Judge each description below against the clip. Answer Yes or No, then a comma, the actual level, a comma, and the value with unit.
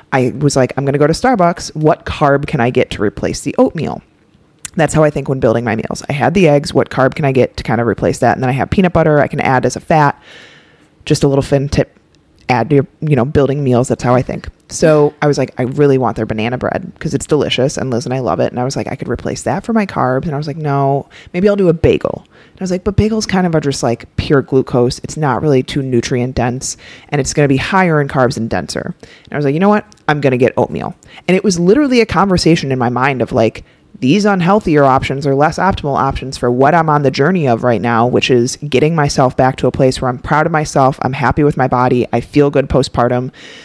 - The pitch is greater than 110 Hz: Yes, medium, 140 Hz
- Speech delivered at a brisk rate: Yes, fast, 270 wpm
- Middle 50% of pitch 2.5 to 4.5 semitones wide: Yes, average, 3.5 semitones